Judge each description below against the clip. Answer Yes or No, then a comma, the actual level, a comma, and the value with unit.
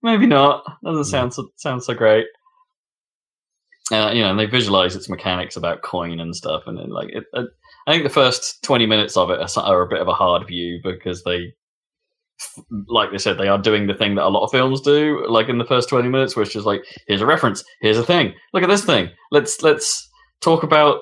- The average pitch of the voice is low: Yes, low, 125 Hz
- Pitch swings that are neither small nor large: No, wide, 8.4 semitones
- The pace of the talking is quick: Yes, fast, 225 wpm